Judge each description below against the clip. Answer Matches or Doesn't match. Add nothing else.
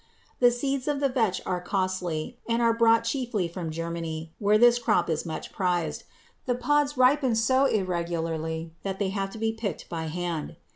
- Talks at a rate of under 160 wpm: Doesn't match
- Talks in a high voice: Matches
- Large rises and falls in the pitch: Matches